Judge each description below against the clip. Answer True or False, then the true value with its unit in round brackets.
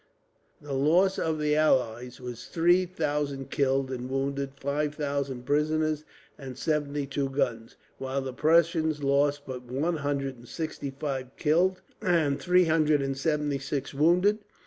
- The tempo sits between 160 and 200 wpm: False (145 wpm)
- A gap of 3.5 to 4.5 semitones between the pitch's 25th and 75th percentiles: False (2.6 semitones)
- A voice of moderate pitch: True (145 Hz)